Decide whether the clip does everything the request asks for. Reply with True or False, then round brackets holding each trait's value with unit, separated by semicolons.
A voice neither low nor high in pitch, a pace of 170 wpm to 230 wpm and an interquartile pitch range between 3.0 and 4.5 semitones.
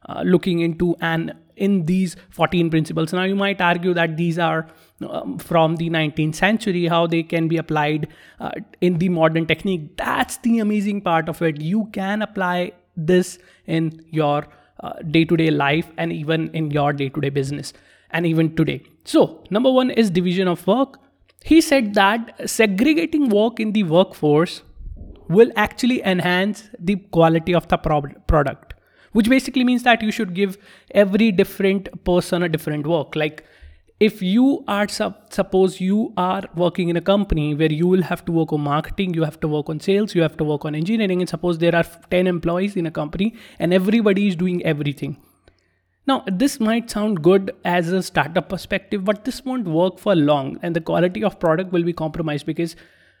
True (175 Hz; 185 wpm; 4.0 semitones)